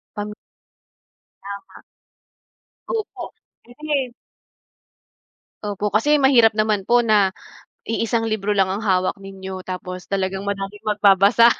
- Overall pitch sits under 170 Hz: No, high, 205 Hz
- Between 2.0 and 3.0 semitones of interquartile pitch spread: Yes, average, 2.7 semitones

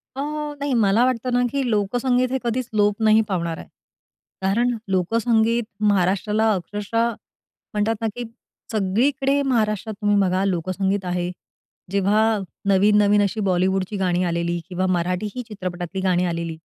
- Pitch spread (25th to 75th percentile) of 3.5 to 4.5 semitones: Yes, average, 3.8 semitones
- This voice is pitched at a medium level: No, high, 205 Hz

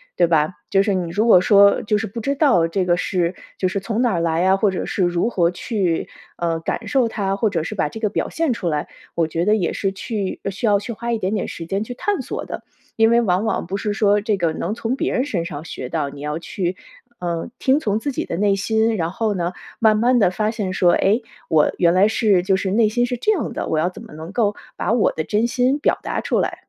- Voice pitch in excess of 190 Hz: Yes, high, 200 Hz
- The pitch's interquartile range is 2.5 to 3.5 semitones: No, average, 4.2 semitones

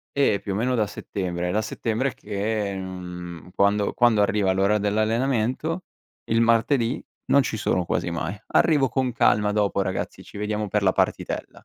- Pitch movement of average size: Yes, average, 3.0 semitones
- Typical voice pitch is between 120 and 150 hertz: No, low, 105 Hz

